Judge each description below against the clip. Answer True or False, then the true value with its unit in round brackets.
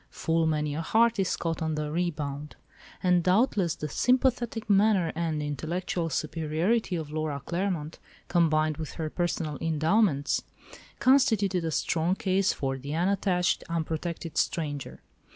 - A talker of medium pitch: True (165 Hz)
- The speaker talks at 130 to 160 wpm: True (135 wpm)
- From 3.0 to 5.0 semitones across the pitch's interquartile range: True (3.5 semitones)